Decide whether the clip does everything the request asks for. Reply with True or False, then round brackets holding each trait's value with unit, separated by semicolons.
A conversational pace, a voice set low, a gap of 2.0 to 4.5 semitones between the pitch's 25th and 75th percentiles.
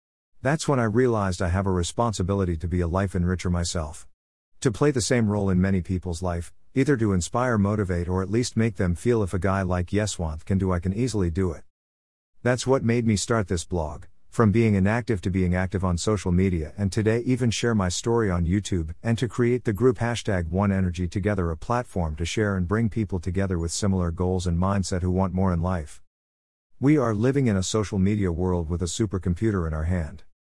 False (215 wpm; 95 Hz; 4.2 semitones)